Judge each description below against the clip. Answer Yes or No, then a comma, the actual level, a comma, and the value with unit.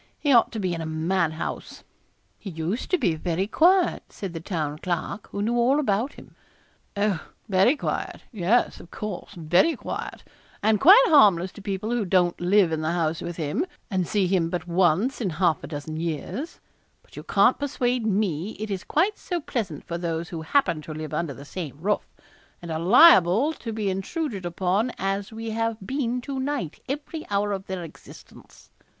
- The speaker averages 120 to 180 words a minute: No, average, 190 wpm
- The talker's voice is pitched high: Yes, high, 195 Hz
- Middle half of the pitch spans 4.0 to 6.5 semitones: Yes, wide, 5.6 semitones